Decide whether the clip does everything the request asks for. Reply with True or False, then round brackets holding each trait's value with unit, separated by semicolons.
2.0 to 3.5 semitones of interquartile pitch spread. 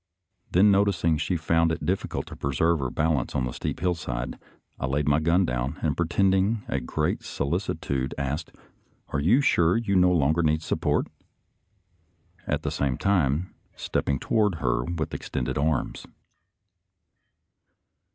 False (4.3 semitones)